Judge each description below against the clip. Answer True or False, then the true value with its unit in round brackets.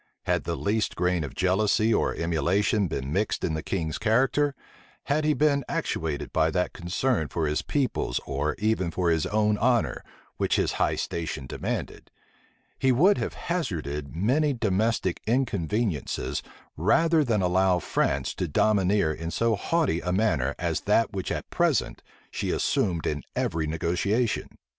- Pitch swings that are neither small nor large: False (5.9 semitones)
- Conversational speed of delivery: True (155 wpm)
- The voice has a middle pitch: False (95 Hz)